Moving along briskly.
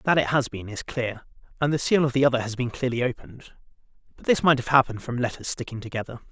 Yes: fast, 240 wpm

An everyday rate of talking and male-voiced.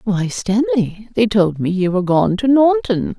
No: average, 190 wpm; female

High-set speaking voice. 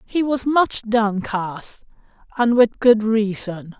Yes: high, 220 Hz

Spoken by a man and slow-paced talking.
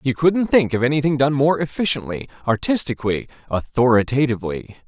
Yes: male; slow, 125 wpm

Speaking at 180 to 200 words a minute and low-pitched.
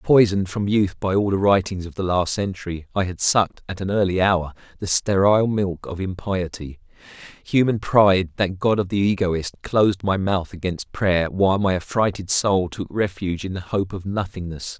Yes: average, 185 wpm; very low, 95 Hz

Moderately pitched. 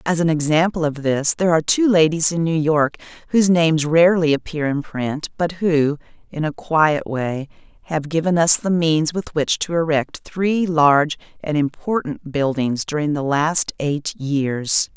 Yes: medium, 155 Hz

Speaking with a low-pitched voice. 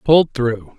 Yes: low, 130 Hz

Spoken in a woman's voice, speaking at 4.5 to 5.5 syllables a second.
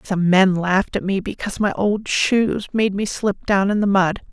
Yes: female; 4.6 syllables/s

